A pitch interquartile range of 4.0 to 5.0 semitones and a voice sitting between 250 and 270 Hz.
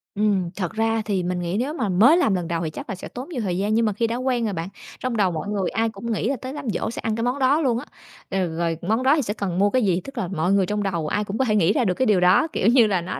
No: average, 4.4 semitones; high, 210 Hz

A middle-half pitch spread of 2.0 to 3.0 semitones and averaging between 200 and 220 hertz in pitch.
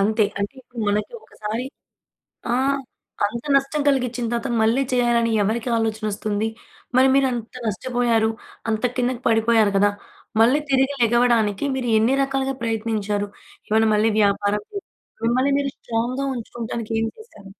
No: narrow, 2.6 semitones; high, 230 Hz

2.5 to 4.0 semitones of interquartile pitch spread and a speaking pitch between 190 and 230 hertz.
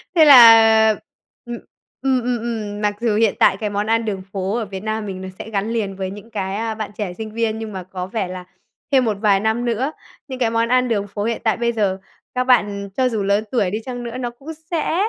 Yes: average, 2.8 semitones; high, 220 Hz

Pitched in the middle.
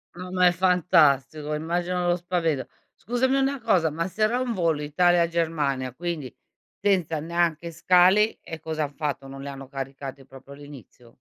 Yes: medium, 165 Hz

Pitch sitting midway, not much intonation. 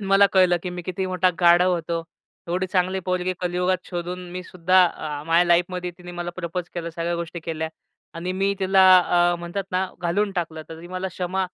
Yes: medium, 180 Hz; narrow, 1.3 semitones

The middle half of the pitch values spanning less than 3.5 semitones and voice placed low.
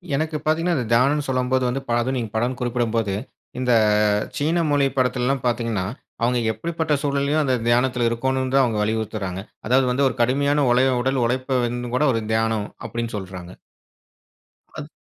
Yes: average, 2.8 semitones; low, 125 Hz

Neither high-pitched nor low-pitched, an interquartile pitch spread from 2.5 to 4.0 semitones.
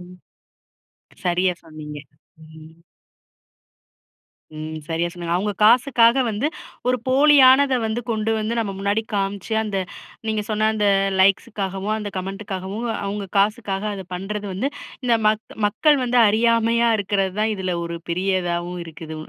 No: high, 205 Hz; average, 3.5 semitones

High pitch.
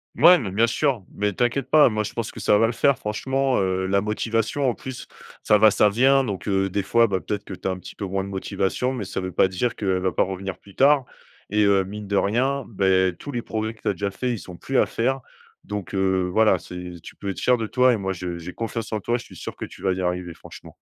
No: low, 105 Hz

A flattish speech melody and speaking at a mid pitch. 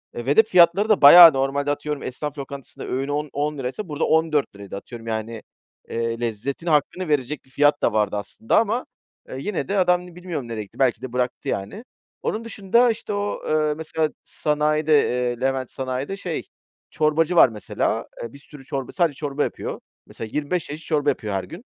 No: average, 4.6 semitones; medium, 145 Hz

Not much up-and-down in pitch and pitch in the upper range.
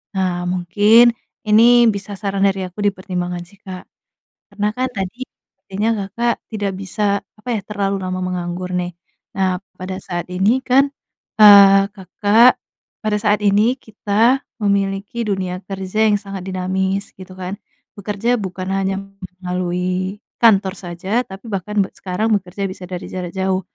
Yes: narrow, 2.1 semitones; high, 195 Hz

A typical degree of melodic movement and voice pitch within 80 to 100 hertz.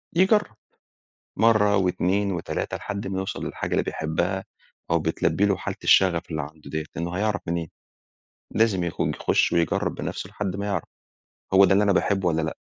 Yes: average, 3.3 semitones; very low, 95 Hz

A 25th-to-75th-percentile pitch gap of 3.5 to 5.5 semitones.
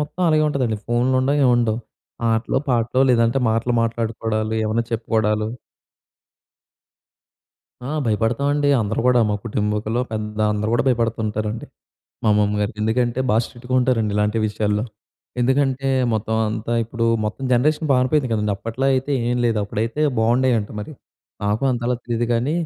No: average, 2.8 semitones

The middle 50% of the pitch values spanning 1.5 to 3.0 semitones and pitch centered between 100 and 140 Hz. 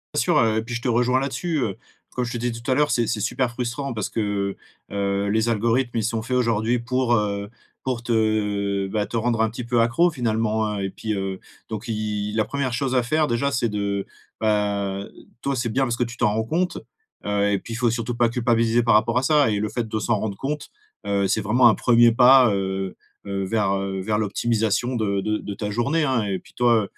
Yes: average, 2.7 semitones; low, 115 Hz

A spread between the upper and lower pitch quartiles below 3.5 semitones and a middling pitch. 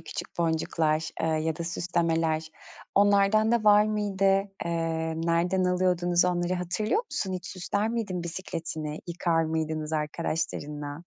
Yes: average, 2.7 semitones; medium, 170 Hz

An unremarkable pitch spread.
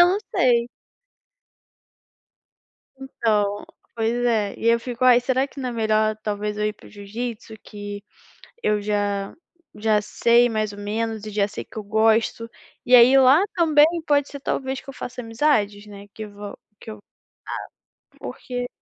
Yes: average, 3.1 semitones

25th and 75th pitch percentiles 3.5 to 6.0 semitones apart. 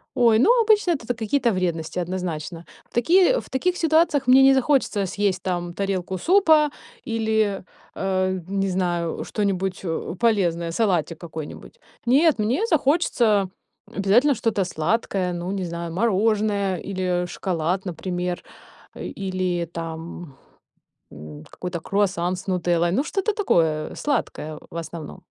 Yes: average, 5.3 semitones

